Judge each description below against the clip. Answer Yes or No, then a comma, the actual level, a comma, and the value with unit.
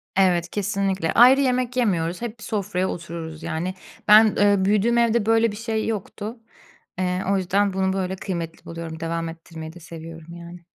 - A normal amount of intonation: Yes, average, 4.4 semitones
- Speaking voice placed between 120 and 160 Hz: No, high, 190 Hz